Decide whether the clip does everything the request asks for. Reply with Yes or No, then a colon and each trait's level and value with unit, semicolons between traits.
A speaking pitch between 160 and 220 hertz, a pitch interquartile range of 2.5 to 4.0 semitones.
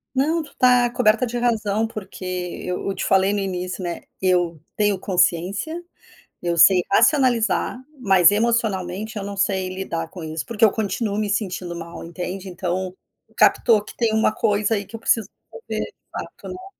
Yes: high, 200 Hz; average, 3.7 semitones